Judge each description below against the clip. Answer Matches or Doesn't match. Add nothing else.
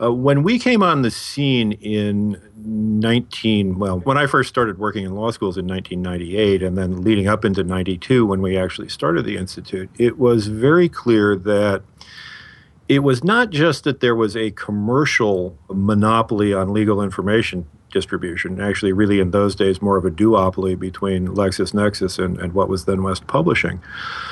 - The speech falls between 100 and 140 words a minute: Doesn't match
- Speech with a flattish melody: Doesn't match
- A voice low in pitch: Matches